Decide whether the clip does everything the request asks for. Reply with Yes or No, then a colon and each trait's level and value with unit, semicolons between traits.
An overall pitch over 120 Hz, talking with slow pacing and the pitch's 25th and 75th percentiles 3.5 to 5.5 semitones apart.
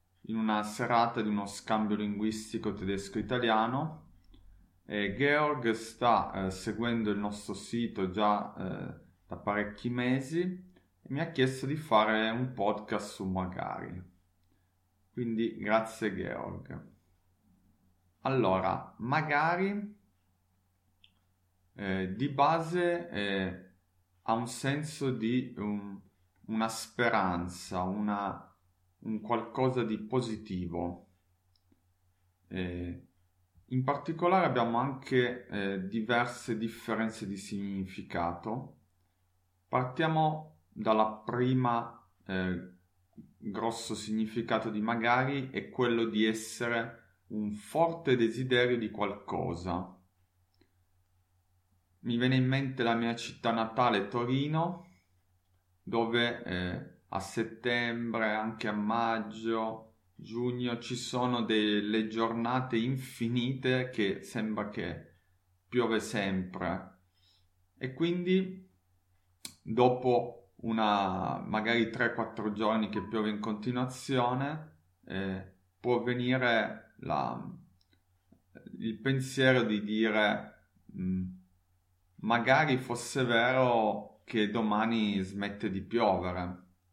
No: low, 110 Hz; slow, 90 wpm; average, 4.4 semitones